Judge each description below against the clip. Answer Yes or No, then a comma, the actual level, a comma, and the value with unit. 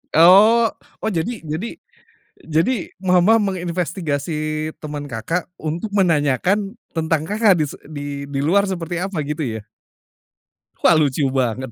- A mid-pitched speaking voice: Yes, medium, 165 Hz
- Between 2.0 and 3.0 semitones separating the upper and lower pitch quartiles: No, average, 4.3 semitones